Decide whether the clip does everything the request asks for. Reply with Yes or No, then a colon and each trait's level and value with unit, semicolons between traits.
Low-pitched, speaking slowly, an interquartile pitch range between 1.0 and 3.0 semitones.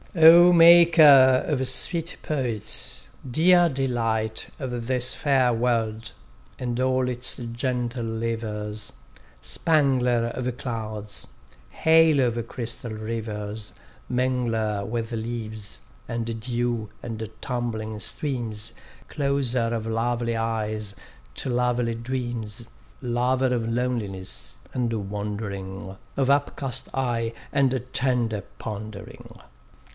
Yes: low, 120 Hz; slow, 100 wpm; average, 2.7 semitones